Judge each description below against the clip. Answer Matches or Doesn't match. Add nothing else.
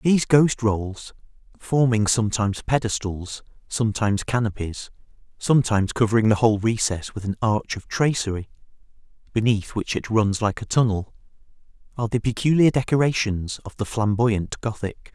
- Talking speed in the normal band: Doesn't match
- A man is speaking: Matches